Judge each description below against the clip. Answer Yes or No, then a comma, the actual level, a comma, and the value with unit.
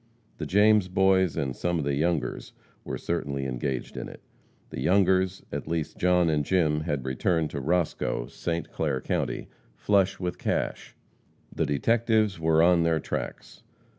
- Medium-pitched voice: No, very low, 85 Hz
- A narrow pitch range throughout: No, average, 4.1 semitones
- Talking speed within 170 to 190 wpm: No, average, 155 wpm